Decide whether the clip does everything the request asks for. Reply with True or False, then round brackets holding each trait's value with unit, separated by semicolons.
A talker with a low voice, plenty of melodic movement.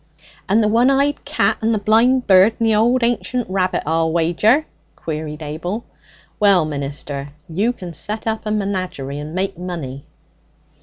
False (195 Hz; 5.7 semitones)